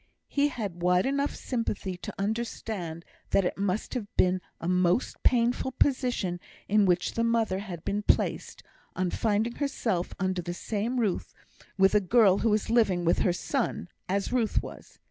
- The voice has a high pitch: Yes, high, 205 Hz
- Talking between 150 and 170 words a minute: Yes, average, 165 wpm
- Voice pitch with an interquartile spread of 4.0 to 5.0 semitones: Yes, average, 4.3 semitones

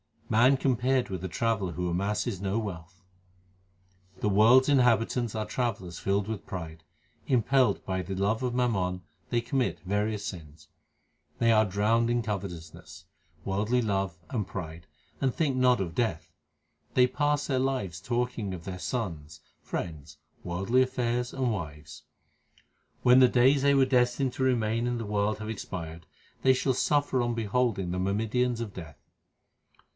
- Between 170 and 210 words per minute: No, average, 155 wpm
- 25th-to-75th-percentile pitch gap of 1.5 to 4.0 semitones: No, average, 5.0 semitones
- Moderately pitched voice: No, low, 110 Hz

